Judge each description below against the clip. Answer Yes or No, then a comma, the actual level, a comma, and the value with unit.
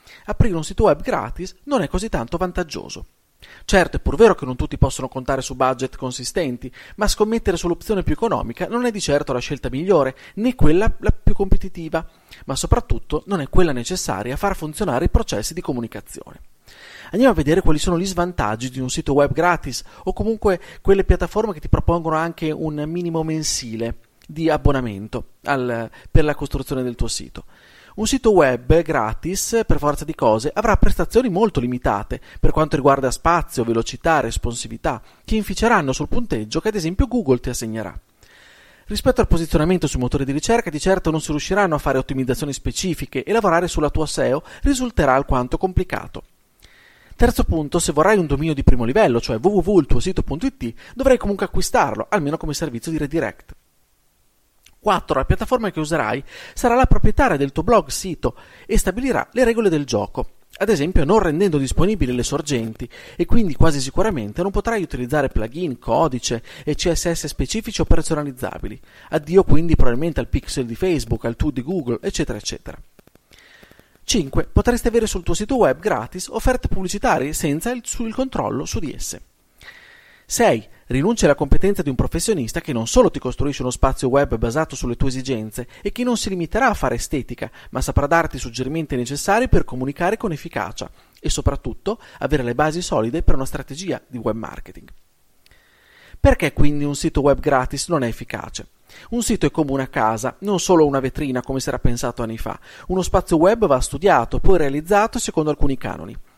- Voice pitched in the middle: Yes, medium, 155 Hz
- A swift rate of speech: Yes, fast, 175 wpm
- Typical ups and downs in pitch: No, wide, 6.5 semitones